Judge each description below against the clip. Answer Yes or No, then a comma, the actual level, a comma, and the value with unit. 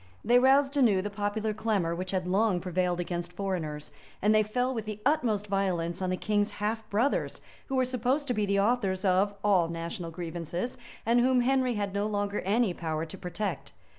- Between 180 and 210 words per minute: Yes, average, 195 wpm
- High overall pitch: Yes, high, 205 Hz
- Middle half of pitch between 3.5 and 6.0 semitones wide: Yes, average, 4.0 semitones